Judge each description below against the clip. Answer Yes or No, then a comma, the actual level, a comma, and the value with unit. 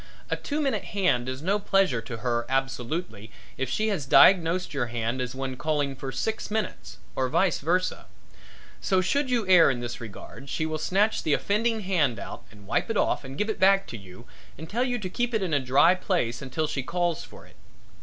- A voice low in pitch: No, medium, 155 Hz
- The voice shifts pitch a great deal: Yes, wide, 7.1 semitones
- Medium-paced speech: No, fast, 215 wpm